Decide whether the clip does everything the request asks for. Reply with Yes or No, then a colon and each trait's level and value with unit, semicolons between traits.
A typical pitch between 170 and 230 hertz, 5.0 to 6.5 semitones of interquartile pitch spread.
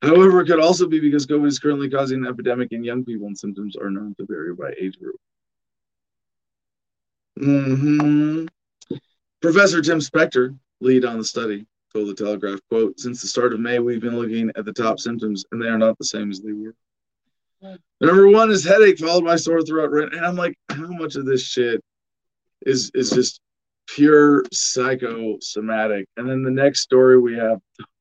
No: low, 125 Hz; average, 5.3 semitones